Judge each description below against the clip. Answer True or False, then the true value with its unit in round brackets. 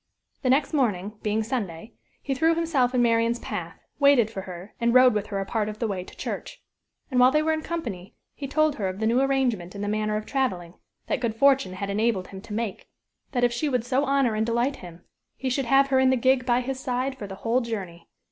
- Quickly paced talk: True (240 wpm)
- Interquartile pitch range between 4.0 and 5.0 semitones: True (4.3 semitones)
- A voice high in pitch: True (235 Hz)